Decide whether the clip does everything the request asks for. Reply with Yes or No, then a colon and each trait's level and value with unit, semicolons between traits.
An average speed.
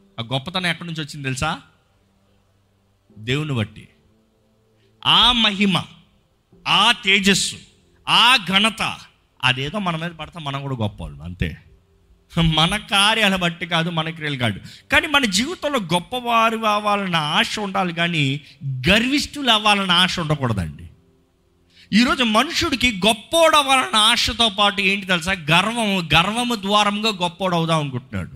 Yes: average, 110 wpm